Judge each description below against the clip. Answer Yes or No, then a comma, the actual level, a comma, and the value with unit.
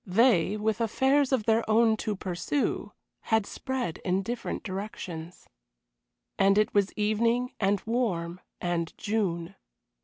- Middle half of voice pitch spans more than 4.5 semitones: No, average, 3.9 semitones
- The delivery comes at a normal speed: No, slow, 125 wpm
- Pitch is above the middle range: Yes, high, 210 Hz